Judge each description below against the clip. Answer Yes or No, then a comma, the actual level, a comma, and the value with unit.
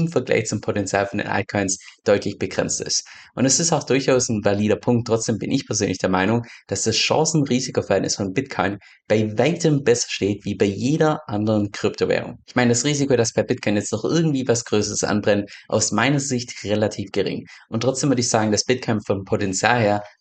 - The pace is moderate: No, fast, 195 wpm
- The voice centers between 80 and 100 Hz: No, low, 115 Hz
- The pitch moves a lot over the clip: No, average, 3.6 semitones